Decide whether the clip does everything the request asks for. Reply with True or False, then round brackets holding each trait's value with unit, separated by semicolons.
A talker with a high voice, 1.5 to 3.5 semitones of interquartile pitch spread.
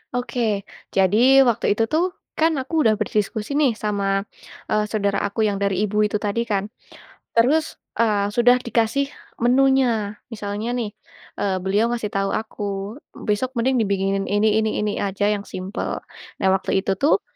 True (215 Hz; 3.2 semitones)